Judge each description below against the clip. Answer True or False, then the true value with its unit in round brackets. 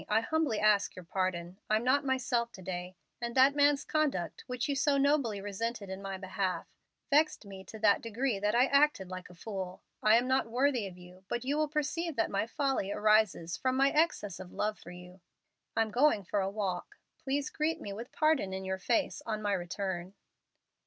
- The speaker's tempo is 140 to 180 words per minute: False (200 wpm)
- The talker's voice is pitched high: True (215 Hz)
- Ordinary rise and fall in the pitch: False (6.0 semitones)